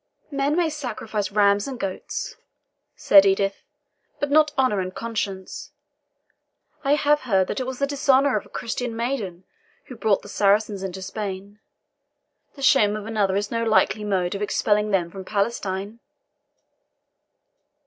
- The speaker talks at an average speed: Yes, average, 150 wpm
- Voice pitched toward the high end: Yes, high, 210 Hz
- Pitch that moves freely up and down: No, average, 4.7 semitones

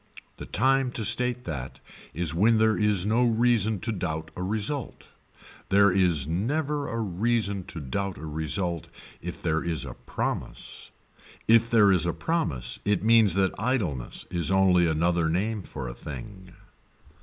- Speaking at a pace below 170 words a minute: Yes, average, 155 wpm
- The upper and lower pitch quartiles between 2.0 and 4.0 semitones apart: No, average, 4.9 semitones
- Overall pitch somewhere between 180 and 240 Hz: No, low, 100 Hz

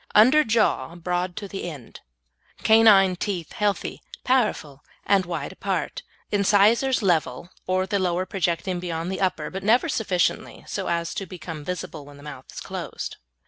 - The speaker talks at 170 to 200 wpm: No, average, 155 wpm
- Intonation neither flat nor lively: Yes, average, 3.2 semitones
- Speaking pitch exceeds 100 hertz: Yes, medium, 185 Hz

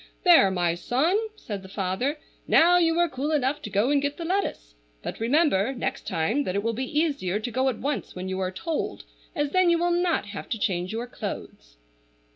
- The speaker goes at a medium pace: No, fast, 215 wpm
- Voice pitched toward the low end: No, very high, 255 Hz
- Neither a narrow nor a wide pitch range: No, wide, 8.5 semitones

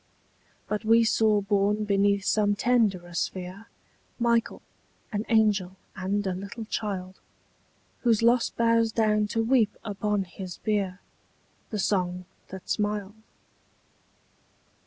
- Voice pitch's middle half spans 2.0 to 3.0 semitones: Yes, narrow, 2.5 semitones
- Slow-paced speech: Yes, slow, 115 wpm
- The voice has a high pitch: Yes, high, 210 Hz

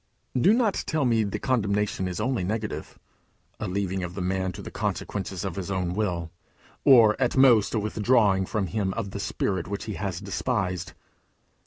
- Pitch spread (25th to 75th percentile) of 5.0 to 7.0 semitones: No, average, 3.1 semitones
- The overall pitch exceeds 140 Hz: No, low, 100 Hz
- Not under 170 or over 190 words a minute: Yes, average, 180 wpm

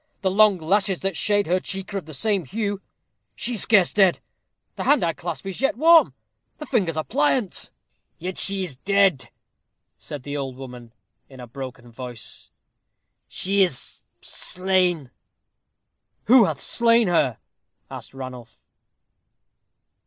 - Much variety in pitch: Yes, wide, 6.7 semitones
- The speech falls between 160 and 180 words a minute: No, average, 145 wpm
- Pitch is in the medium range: Yes, medium, 180 Hz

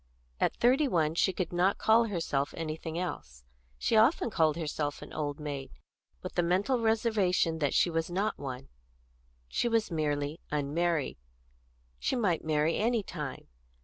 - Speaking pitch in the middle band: Yes, medium, 170 Hz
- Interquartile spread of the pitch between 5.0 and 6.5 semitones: Yes, wide, 5.6 semitones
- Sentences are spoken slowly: No, average, 150 wpm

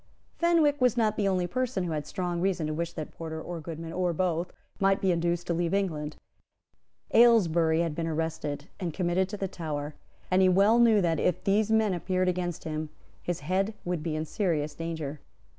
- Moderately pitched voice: Yes, medium, 175 Hz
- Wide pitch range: No, average, 3.3 semitones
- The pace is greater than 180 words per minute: Yes, average, 195 wpm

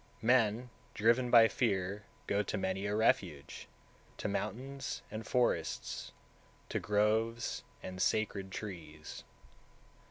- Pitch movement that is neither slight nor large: Yes, average, 3.1 semitones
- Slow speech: Yes, slow, 115 wpm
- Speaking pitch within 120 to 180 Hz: No, low, 105 Hz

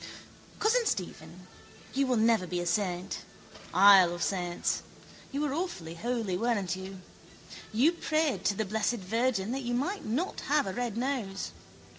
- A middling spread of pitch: No, wide, 6.0 semitones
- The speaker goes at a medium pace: Yes, average, 155 wpm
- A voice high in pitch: Yes, high, 220 Hz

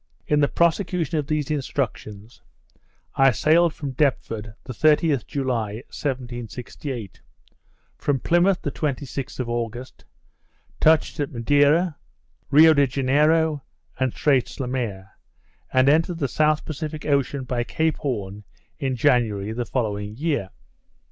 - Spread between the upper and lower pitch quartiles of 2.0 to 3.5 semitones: No, average, 4.2 semitones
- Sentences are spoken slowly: Yes, slow, 125 wpm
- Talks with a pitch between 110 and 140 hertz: Yes, low, 135 Hz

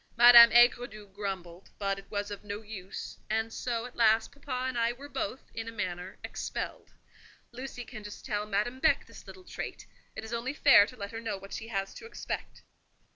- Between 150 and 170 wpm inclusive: No, average, 200 wpm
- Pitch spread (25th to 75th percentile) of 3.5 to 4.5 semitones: No, average, 3.1 semitones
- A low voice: No, high, 225 Hz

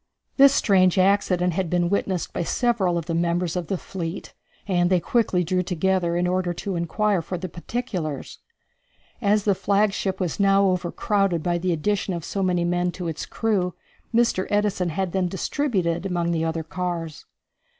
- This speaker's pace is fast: No, average, 170 wpm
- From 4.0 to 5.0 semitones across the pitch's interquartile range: No, narrow, 2.4 semitones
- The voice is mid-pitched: Yes, medium, 180 Hz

